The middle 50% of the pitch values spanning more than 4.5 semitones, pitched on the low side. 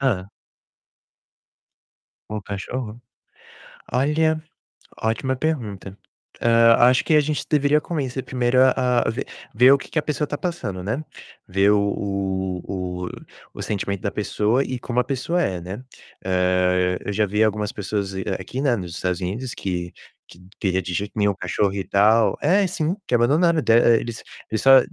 Yes: wide, 5.6 semitones; low, 115 Hz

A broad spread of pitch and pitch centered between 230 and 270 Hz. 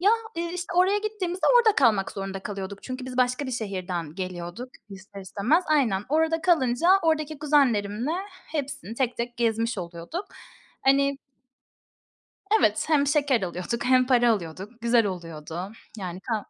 Yes: wide, 7.2 semitones; high, 240 Hz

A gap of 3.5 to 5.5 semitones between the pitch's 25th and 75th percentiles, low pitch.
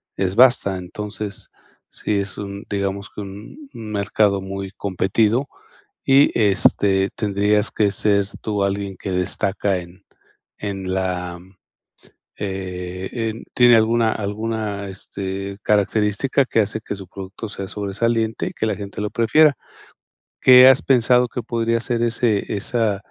No: narrow, 2.6 semitones; low, 105 Hz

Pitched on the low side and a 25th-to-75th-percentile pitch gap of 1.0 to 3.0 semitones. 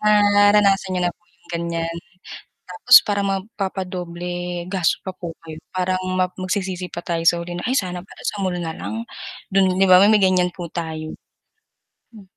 No: medium, 185 Hz; narrow, 2.4 semitones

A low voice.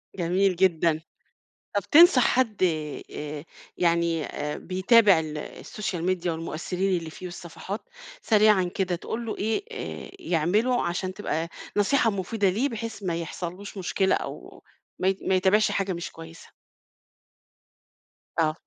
No: medium, 185 Hz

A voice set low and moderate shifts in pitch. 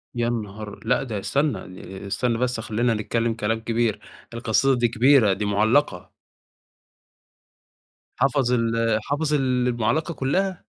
Yes: low, 120 Hz; average, 3.2 semitones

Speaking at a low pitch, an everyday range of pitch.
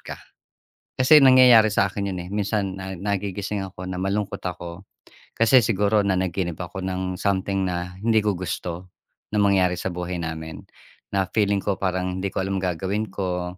No: very low, 95 Hz; narrow, 2.0 semitones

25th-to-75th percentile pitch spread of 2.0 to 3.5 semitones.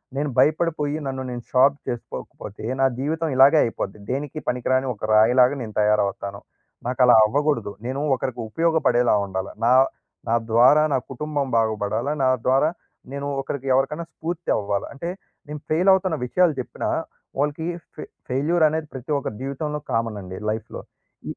No: average, 4.8 semitones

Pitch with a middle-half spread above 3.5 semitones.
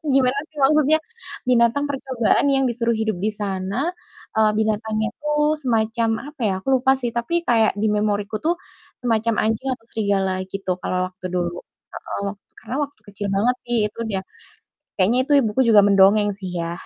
Yes: average, 4.3 semitones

